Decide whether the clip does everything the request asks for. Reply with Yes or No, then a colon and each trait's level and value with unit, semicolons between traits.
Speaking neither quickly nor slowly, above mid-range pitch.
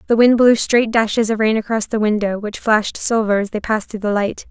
No: fast, 255 wpm; high, 220 Hz